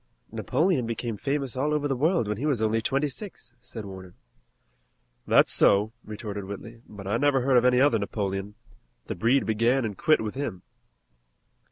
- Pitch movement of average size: Yes, average, 4.7 semitones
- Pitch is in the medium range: No, low, 115 Hz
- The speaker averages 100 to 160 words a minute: No, average, 175 wpm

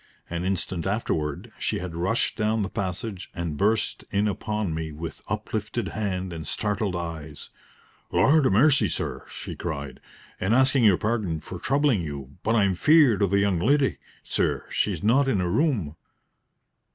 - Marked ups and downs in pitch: No, average, 4.8 semitones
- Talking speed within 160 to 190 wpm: Yes, average, 165 wpm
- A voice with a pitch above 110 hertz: No, low, 100 Hz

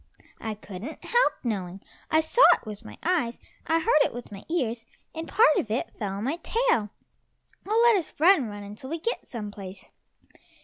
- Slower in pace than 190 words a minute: No, average, 195 wpm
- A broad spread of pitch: Yes, wide, 8.1 semitones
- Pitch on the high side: Yes, high, 245 Hz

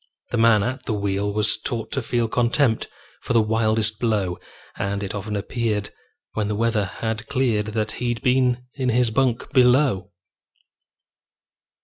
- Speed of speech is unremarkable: Yes, average, 150 wpm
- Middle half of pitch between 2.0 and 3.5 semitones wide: Yes, average, 2.7 semitones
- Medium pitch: No, low, 110 Hz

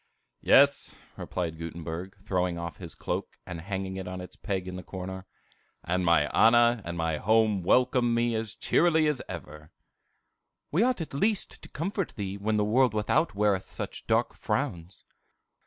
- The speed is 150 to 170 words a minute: Yes, average, 165 wpm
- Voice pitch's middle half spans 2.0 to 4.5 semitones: No, average, 4.9 semitones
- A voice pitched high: No, very low, 95 Hz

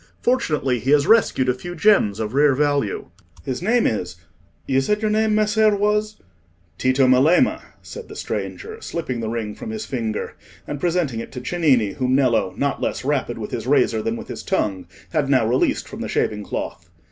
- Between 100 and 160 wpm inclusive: No, average, 185 wpm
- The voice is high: No, low, 135 Hz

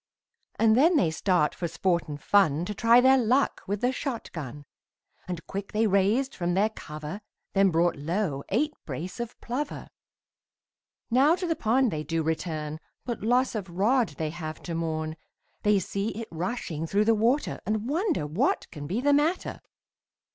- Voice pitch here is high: Yes, high, 200 Hz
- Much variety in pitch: Yes, wide, 7.0 semitones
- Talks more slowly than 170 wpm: No, average, 175 wpm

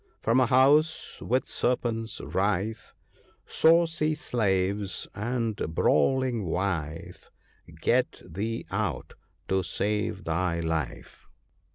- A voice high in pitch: No, low, 105 Hz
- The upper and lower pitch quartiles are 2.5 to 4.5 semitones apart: No, wide, 5.4 semitones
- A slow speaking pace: Yes, slow, 95 wpm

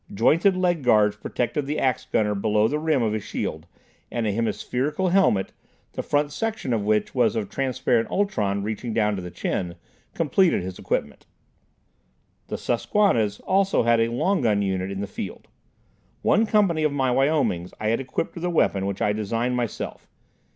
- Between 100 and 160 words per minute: No, average, 175 wpm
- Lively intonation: Yes, wide, 6.6 semitones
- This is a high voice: No, low, 115 Hz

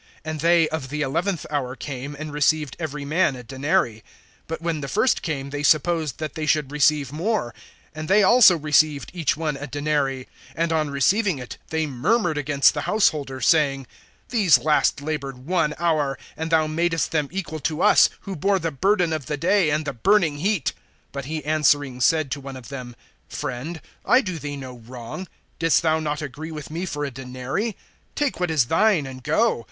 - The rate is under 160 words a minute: No, average, 190 wpm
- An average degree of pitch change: Yes, average, 3.1 semitones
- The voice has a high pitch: No, medium, 150 Hz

